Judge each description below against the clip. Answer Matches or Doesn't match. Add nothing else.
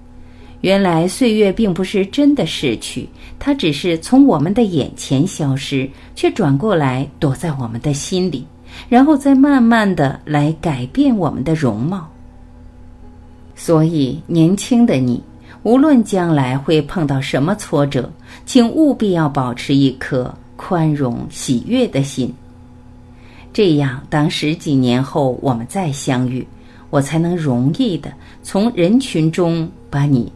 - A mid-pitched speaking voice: Matches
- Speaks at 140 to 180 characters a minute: Doesn't match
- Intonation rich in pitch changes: Matches